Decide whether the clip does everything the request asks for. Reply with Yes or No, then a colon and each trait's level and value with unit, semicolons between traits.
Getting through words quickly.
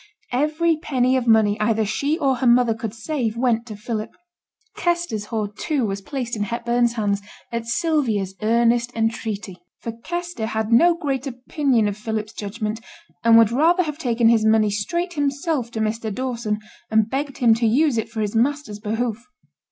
No: average, 175 wpm